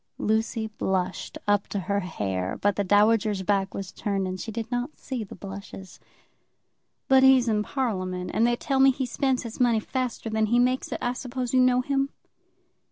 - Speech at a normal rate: Yes, average, 190 wpm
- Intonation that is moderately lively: Yes, average, 4.2 semitones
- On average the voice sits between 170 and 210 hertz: No, high, 220 Hz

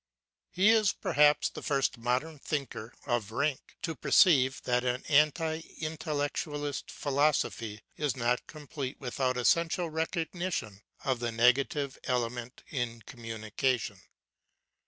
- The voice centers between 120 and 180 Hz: Yes, low, 135 Hz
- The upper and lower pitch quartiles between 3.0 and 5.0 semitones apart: Yes, average, 3.9 semitones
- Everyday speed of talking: No, slow, 115 wpm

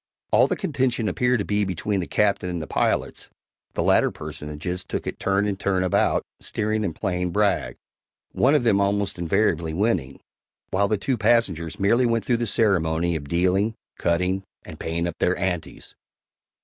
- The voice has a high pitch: No, very low, 95 Hz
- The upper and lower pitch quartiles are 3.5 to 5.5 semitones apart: Yes, average, 3.8 semitones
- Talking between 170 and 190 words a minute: Yes, average, 175 wpm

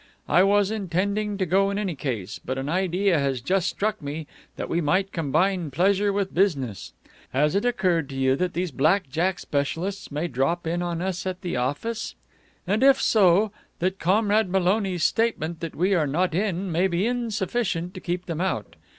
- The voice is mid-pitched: Yes, medium, 180 Hz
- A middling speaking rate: Yes, average, 185 wpm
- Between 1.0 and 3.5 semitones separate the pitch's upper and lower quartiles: No, average, 3.9 semitones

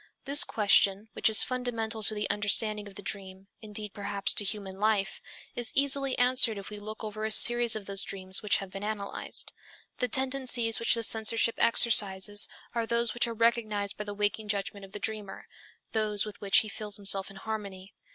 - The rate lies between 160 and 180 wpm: No, average, 190 wpm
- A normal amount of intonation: No, narrow, 2.2 semitones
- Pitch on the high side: Yes, high, 210 Hz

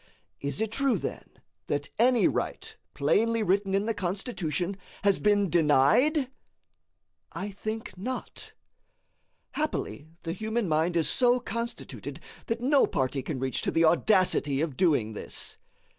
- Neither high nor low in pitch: No, high, 195 Hz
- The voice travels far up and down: Yes, wide, 6.3 semitones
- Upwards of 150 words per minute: No, slow, 135 wpm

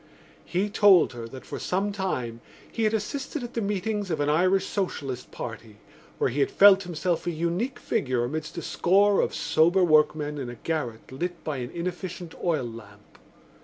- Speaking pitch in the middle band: Yes, medium, 170 Hz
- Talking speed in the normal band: Yes, average, 180 wpm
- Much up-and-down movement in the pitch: Yes, wide, 6.5 semitones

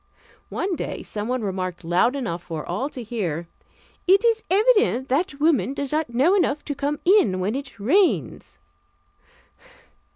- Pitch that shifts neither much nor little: No, wide, 8.7 semitones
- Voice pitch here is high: Yes, very high, 265 Hz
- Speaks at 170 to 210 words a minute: No, average, 150 wpm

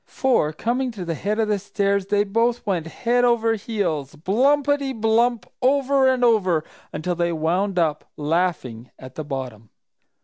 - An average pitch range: No, wide, 6.6 semitones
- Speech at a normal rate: Yes, average, 160 wpm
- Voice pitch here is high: Yes, high, 200 Hz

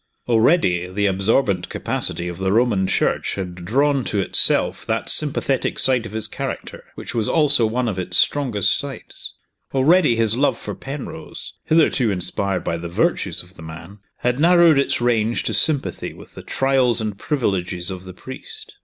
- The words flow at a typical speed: Yes, average, 170 wpm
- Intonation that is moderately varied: No, wide, 6.3 semitones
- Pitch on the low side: Yes, low, 110 Hz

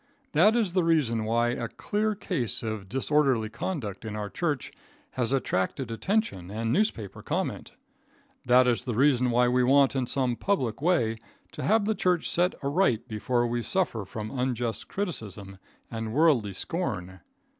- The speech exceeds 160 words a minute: No, average, 155 wpm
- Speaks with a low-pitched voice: Yes, low, 125 Hz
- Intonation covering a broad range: Yes, wide, 6.6 semitones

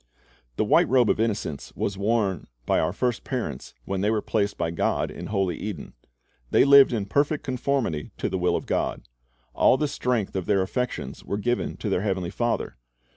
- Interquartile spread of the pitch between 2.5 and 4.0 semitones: No, average, 4.6 semitones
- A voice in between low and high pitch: No, low, 105 Hz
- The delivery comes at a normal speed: Yes, average, 190 wpm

